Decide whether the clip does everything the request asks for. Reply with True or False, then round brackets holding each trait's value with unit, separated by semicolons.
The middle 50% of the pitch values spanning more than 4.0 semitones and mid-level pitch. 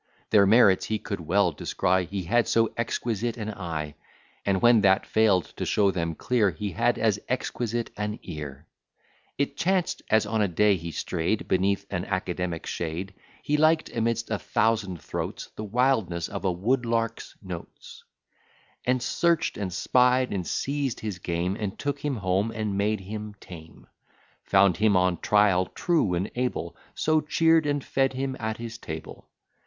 False (4.4 semitones; 105 Hz)